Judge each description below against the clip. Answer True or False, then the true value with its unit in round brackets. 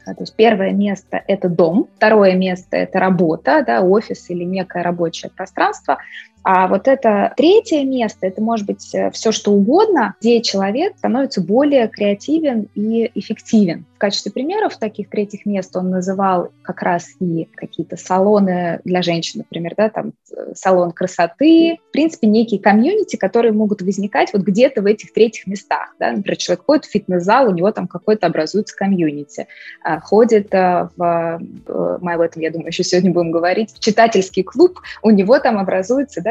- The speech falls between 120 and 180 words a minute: True (160 wpm)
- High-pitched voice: True (205 Hz)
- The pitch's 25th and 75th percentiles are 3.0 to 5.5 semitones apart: True (3.8 semitones)